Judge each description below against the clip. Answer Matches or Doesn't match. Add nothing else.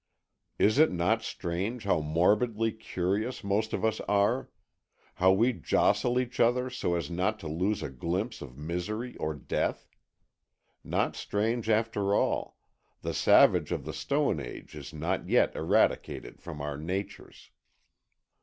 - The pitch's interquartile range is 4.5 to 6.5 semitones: Matches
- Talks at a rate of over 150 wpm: Doesn't match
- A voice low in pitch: Matches